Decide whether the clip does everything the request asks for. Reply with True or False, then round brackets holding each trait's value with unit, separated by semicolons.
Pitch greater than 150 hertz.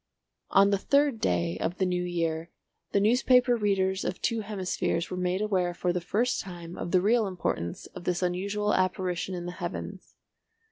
True (185 Hz)